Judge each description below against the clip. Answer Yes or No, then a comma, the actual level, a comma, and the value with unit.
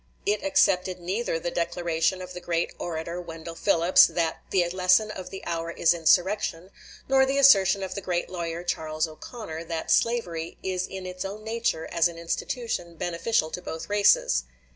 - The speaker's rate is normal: Yes, average, 170 wpm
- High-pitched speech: No, medium, 180 Hz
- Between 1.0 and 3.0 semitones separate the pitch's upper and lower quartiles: Yes, average, 2.7 semitones